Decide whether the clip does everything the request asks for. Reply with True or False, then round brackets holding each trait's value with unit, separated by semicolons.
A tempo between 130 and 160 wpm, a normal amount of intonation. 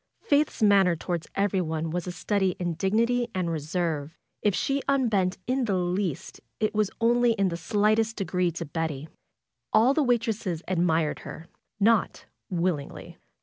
True (150 wpm; 4.6 semitones)